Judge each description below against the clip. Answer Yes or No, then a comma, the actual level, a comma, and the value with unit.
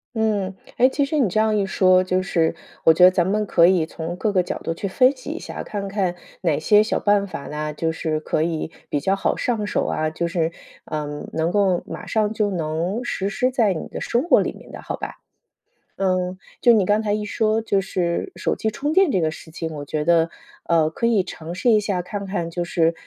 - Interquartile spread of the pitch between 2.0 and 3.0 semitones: No, average, 4.4 semitones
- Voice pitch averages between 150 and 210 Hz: Yes, medium, 185 Hz